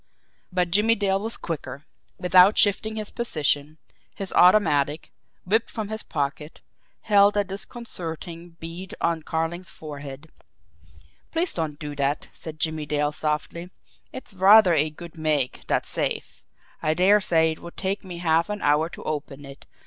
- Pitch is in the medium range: Yes, medium, 170 Hz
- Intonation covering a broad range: No, average, 4.4 semitones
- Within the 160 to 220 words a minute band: No, average, 150 wpm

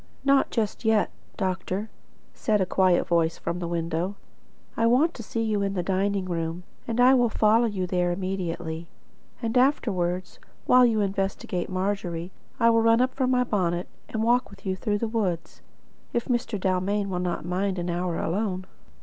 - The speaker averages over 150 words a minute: Yes, average, 175 wpm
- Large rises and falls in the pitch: No, average, 4.2 semitones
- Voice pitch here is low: No, high, 195 Hz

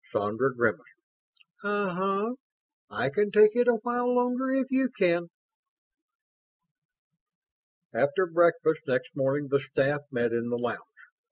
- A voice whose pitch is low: No, medium, 175 Hz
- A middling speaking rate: No, slow, 125 wpm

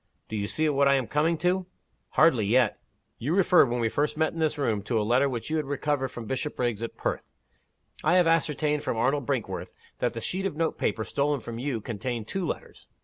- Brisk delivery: Yes, fast, 215 wpm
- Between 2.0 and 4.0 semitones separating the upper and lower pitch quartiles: No, average, 5.0 semitones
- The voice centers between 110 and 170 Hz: Yes, medium, 140 Hz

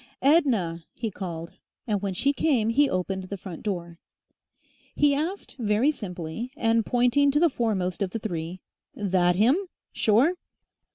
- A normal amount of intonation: No, wide, 6.8 semitones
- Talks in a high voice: Yes, high, 215 Hz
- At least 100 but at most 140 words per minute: No, average, 150 wpm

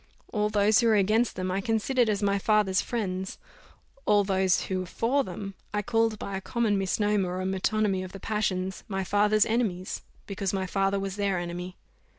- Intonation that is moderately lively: No, narrow, 2.2 semitones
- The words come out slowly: No, average, 185 wpm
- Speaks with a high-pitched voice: Yes, high, 200 Hz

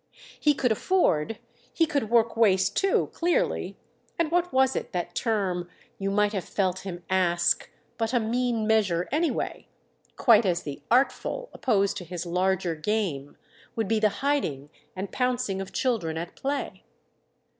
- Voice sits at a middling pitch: No, high, 210 Hz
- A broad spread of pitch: Yes, wide, 5.8 semitones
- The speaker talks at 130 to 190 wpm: Yes, average, 150 wpm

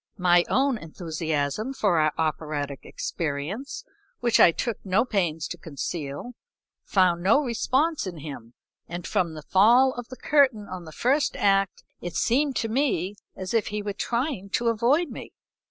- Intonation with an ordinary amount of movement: No, wide, 6.9 semitones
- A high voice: Yes, high, 195 Hz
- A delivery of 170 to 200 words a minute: No, average, 160 wpm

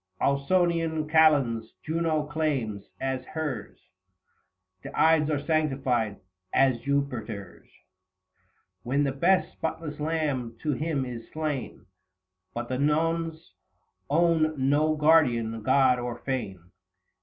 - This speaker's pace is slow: Yes, slow, 110 wpm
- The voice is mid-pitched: Yes, medium, 145 Hz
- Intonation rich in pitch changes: No, average, 4.2 semitones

